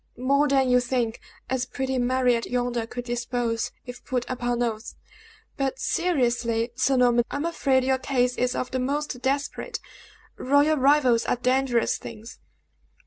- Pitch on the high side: Yes, very high, 250 Hz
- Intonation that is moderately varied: No, narrow, 1.8 semitones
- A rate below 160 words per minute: Yes, average, 150 wpm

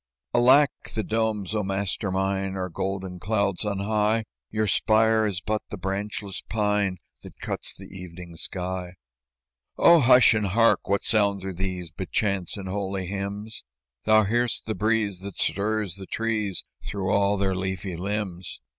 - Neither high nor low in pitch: No, low, 100 Hz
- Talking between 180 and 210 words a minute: No, average, 155 wpm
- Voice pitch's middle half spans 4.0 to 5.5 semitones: No, narrow, 2.4 semitones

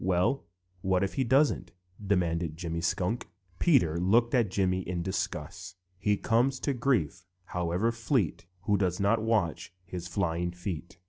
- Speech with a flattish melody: No, average, 4.6 semitones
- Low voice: Yes, very low, 95 Hz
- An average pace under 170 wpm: Yes, average, 140 wpm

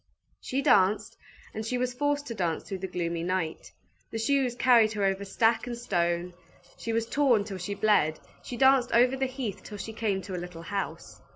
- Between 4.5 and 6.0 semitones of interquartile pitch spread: Yes, average, 4.8 semitones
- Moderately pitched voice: No, high, 215 Hz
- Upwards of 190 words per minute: Yes, average, 200 wpm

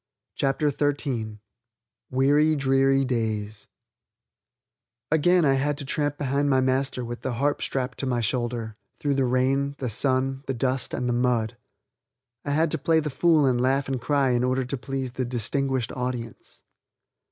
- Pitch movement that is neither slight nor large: No, narrow, 2.3 semitones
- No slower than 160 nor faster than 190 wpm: Yes, average, 165 wpm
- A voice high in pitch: No, low, 130 Hz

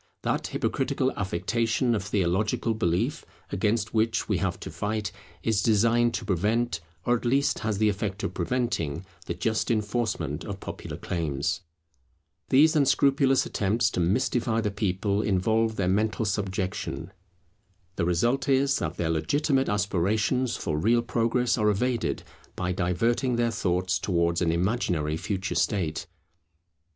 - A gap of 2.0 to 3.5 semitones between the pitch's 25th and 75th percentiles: No, average, 4.5 semitones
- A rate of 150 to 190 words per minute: No, average, 140 wpm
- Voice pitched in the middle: No, low, 105 Hz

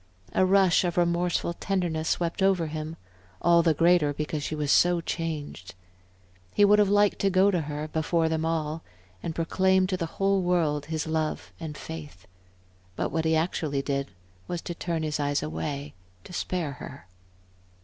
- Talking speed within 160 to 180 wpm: Yes, average, 170 wpm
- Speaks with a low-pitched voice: No, medium, 165 Hz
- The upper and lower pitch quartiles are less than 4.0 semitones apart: Yes, average, 2.8 semitones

